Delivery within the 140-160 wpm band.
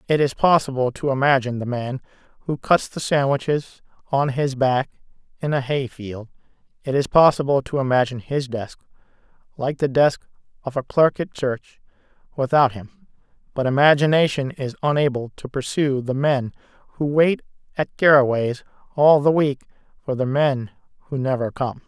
Yes: average, 150 wpm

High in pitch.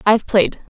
Yes: high, 210 Hz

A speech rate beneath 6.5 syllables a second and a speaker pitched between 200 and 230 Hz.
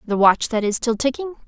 No: 5.7 syllables/s; high, 240 Hz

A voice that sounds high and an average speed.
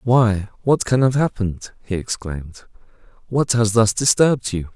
No: low, 110 Hz; average, 150 wpm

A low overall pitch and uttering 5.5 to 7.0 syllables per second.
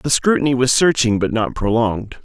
Yes: low, 120 Hz; 5.6 syllables/s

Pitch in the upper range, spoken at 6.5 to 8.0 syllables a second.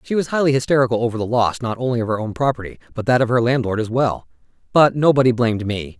No: low, 120 Hz; 6.8 syllables/s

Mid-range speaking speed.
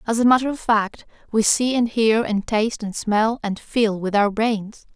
No: fast, 220 wpm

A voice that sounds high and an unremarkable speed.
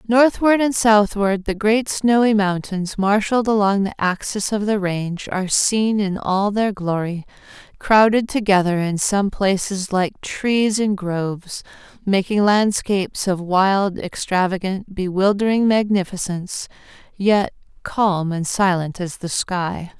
No: high, 200 Hz; slow, 130 wpm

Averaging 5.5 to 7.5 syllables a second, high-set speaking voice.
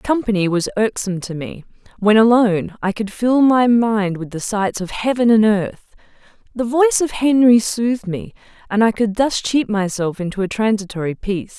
No: 5.1 syllables/s; high, 215 Hz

